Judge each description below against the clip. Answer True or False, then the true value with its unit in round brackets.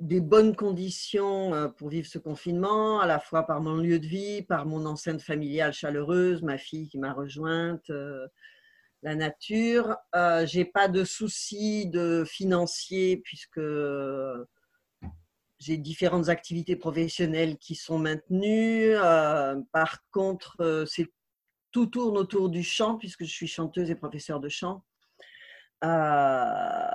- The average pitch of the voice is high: False (170 Hz)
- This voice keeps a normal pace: False (140 wpm)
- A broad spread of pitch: False (4.0 semitones)